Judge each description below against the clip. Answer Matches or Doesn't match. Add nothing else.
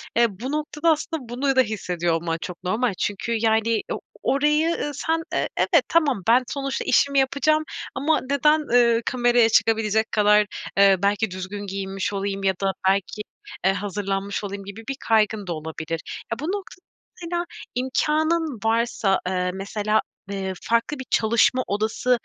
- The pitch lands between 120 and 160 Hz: Doesn't match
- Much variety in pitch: Matches